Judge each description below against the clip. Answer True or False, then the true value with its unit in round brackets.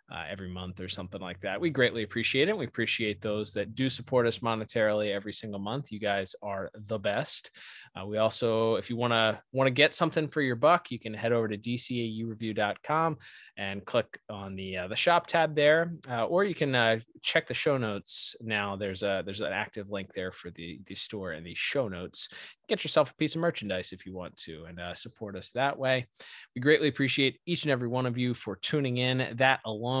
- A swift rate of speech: True (220 wpm)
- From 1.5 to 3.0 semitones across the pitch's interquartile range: False (4.6 semitones)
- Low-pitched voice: True (115 Hz)